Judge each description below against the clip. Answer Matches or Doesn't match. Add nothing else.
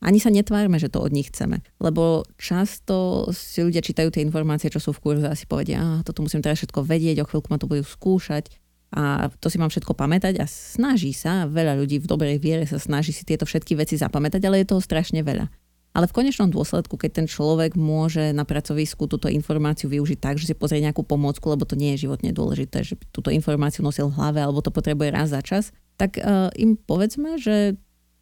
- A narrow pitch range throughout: Doesn't match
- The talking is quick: Matches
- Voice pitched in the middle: Matches